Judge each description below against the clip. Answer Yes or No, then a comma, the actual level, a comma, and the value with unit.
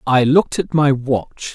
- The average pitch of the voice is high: No, medium, 140 Hz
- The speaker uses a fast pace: No, average, 195 wpm